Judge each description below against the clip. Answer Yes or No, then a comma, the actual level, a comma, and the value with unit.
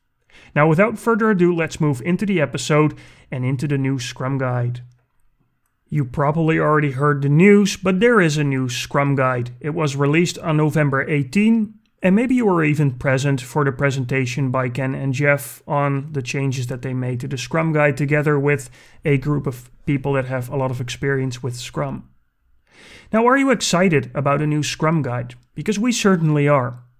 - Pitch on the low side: No, medium, 145 Hz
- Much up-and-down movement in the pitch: No, average, 3.4 semitones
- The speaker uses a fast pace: No, average, 185 wpm